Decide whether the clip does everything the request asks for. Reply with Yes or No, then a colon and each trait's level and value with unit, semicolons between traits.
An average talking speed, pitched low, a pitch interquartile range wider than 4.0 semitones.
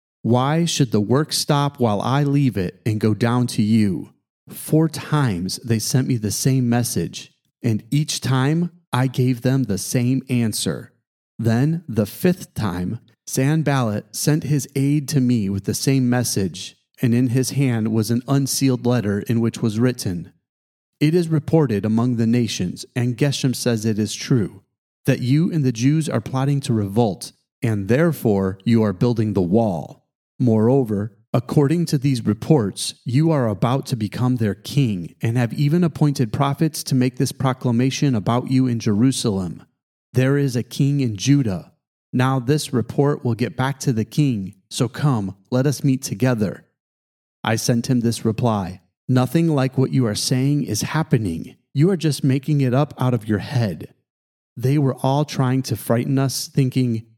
No: average, 170 wpm; low, 125 Hz; average, 3.7 semitones